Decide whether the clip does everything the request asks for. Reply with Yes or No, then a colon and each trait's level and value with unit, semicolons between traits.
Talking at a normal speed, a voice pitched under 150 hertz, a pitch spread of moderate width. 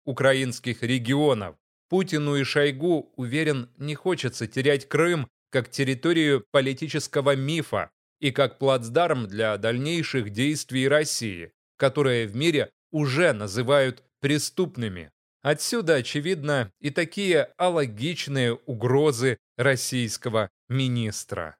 No: slow, 95 wpm; medium, 140 Hz; average, 3.4 semitones